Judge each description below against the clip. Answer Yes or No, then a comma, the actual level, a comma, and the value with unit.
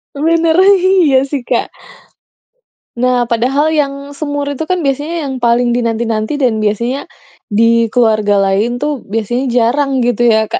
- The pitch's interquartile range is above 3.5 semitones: Yes, average, 3.9 semitones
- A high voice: Yes, very high, 250 Hz